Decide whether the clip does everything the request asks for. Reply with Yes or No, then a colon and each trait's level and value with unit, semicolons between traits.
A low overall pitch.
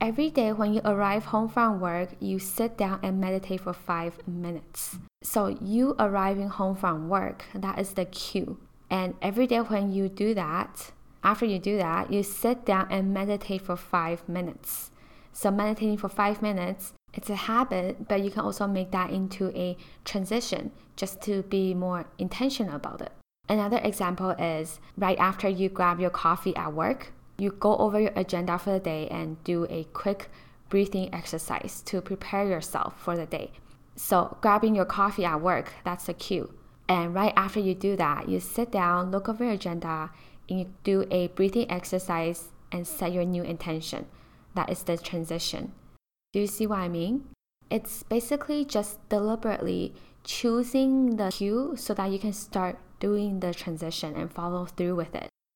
No: high, 190 Hz